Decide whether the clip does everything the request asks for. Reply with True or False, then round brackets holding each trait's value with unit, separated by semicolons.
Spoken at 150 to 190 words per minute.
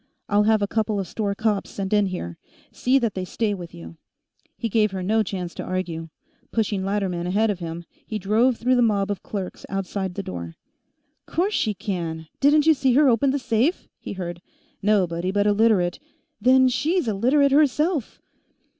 False (200 wpm)